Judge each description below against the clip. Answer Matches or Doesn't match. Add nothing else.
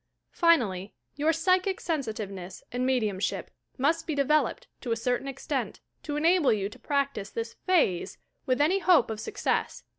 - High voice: Matches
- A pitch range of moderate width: Doesn't match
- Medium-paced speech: Matches